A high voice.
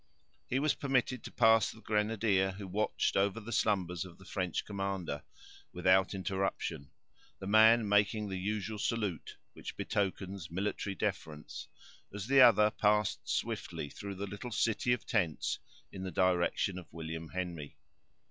No: low, 100 Hz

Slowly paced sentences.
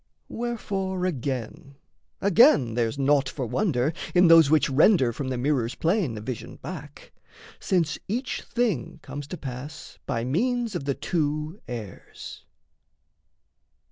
Yes: slow, 130 wpm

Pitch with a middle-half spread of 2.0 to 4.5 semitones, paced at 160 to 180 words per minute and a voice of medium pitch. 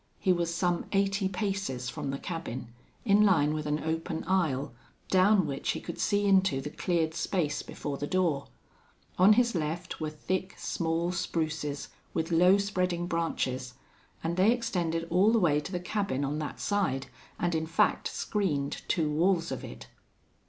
Yes: average, 4.1 semitones; average, 165 wpm; medium, 170 Hz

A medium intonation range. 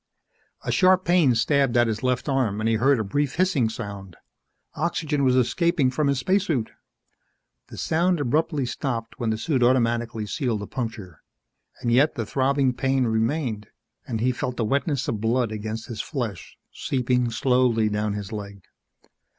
Yes: average, 3.9 semitones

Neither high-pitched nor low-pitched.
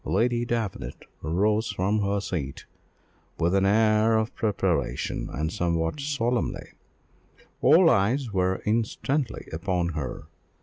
No: low, 105 Hz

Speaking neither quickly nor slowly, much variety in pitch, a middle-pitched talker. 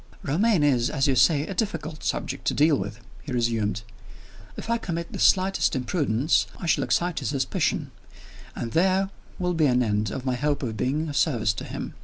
Yes: average, 195 wpm; wide, 5.9 semitones; medium, 145 Hz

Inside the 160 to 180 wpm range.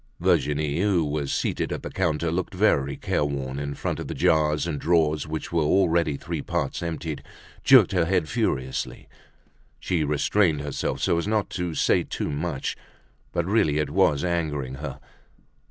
Yes: average, 165 wpm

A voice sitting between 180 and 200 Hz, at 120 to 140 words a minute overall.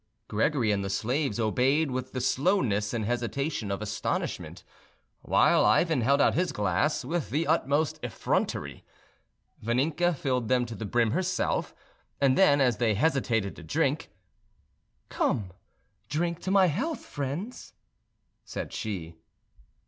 No: low, 130 Hz; slow, 135 wpm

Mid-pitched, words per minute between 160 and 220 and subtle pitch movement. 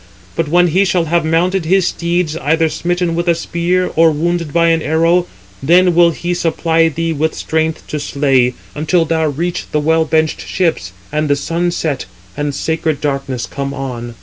Yes: medium, 160 Hz; average, 180 wpm; narrow, 2.3 semitones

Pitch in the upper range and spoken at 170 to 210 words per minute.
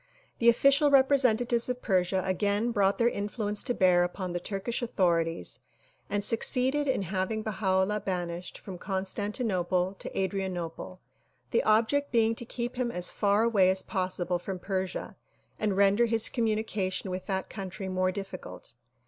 No: high, 200 Hz; average, 150 wpm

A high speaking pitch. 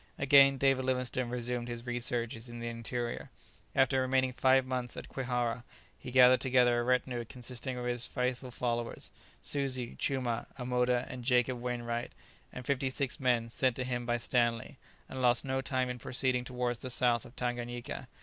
No: low, 125 Hz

